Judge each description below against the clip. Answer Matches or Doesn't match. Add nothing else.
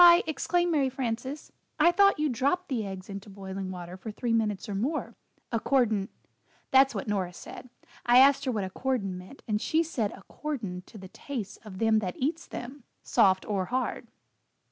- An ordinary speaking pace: Matches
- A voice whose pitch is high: Matches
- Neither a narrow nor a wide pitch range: Doesn't match